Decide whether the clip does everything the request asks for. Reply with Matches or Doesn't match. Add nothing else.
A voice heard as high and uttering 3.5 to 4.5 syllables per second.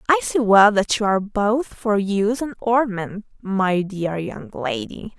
Matches